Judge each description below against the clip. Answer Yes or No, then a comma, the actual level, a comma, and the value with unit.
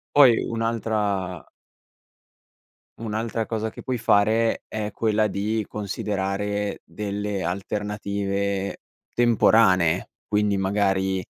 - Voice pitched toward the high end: No, low, 105 Hz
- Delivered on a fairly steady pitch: Yes, narrow, 2.0 semitones